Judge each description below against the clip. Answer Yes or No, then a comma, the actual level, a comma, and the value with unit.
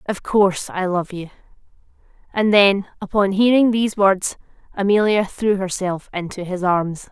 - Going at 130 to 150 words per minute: Yes, average, 145 wpm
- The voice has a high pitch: Yes, high, 195 Hz